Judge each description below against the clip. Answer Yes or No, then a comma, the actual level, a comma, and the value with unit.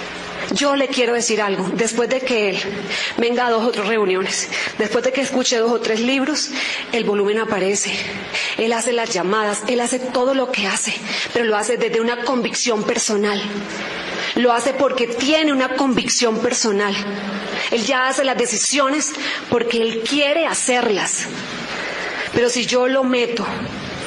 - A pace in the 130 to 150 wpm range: No, average, 160 wpm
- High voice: Yes, high, 235 Hz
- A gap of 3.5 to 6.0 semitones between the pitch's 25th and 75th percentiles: No, average, 3.1 semitones